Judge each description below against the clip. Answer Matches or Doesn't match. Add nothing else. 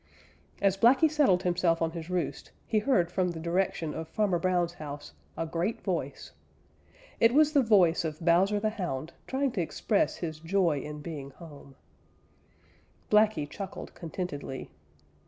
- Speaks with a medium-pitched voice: Matches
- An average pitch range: Matches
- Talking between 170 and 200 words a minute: Doesn't match